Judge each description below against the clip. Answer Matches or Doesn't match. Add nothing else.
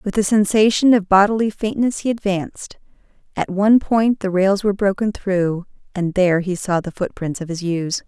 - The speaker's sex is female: Matches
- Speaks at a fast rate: Doesn't match